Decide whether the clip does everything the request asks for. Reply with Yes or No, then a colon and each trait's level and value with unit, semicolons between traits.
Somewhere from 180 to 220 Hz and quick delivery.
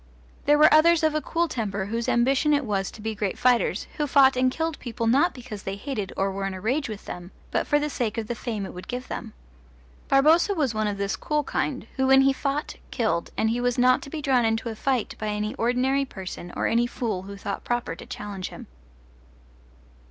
No: high, 240 Hz; fast, 230 wpm